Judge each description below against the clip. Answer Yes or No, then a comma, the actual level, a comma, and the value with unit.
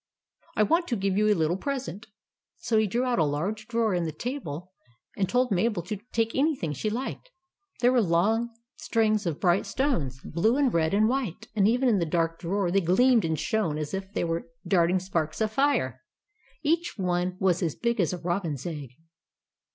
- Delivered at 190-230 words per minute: Yes, average, 200 wpm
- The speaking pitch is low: No, high, 195 Hz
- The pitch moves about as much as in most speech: No, wide, 5.7 semitones